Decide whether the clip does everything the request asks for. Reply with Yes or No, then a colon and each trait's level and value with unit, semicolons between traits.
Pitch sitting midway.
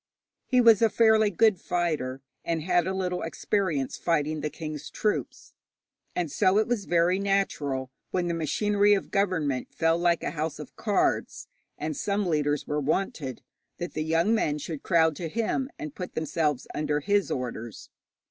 Yes: medium, 170 Hz